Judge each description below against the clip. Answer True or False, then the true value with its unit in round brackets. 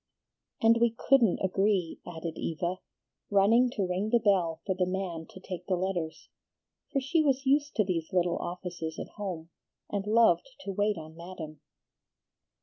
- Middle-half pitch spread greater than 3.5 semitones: True (4.0 semitones)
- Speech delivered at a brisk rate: False (160 wpm)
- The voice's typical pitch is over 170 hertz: True (190 Hz)